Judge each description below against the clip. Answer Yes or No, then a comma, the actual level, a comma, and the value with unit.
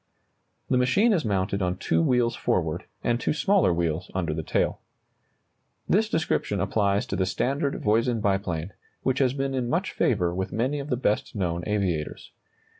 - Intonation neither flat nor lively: No, wide, 6.2 semitones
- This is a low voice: Yes, low, 105 Hz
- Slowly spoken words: No, average, 175 wpm